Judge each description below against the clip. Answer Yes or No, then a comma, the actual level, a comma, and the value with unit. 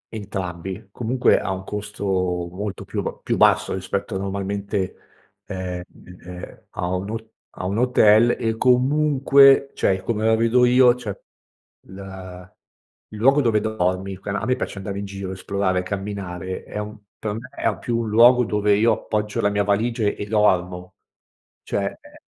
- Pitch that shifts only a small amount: No, average, 3.1 semitones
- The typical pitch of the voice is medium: No, low, 105 Hz